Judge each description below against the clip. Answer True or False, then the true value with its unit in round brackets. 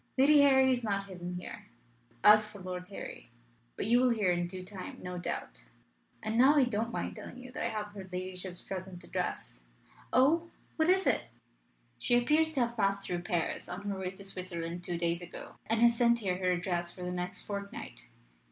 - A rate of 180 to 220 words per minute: True (200 wpm)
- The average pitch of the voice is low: False (195 Hz)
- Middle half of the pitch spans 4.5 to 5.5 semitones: True (4.8 semitones)